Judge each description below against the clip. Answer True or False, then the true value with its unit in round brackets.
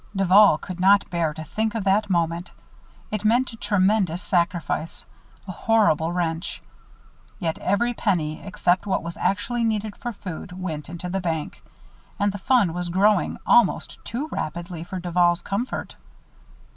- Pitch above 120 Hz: True (185 Hz)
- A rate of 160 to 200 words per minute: False (150 wpm)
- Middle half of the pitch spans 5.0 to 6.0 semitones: False (3.5 semitones)